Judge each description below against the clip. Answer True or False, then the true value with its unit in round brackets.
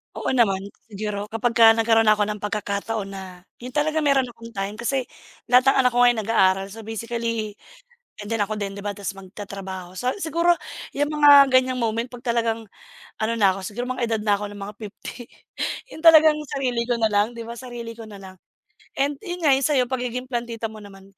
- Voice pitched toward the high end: True (230 Hz)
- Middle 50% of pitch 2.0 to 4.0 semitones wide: True (3.6 semitones)